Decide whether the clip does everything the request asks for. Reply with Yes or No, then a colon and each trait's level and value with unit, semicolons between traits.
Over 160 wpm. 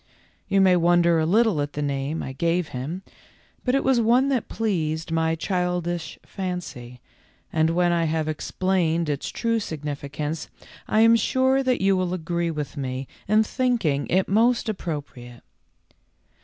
No: average, 155 wpm